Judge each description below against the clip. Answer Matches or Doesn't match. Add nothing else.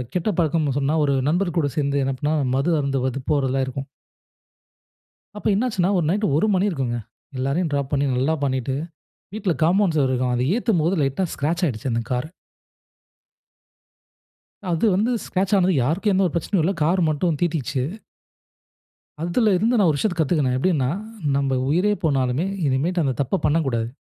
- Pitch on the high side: Doesn't match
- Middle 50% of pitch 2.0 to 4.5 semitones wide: Doesn't match